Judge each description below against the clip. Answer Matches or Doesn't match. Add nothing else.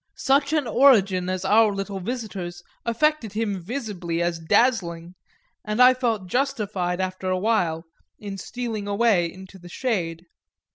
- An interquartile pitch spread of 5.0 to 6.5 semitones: Doesn't match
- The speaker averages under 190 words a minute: Matches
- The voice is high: Matches